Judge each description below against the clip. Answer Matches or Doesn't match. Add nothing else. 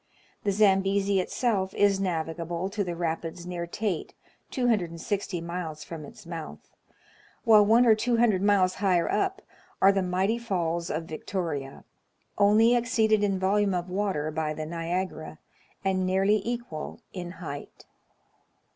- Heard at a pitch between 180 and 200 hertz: Matches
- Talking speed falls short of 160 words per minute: Matches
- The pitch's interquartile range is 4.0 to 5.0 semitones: Doesn't match